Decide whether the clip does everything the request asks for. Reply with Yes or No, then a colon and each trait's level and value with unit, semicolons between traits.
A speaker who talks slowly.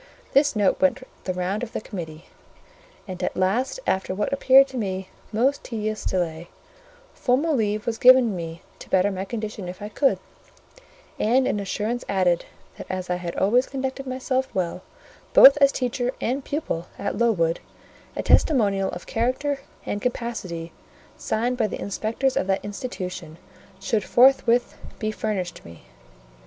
No: average, 155 wpm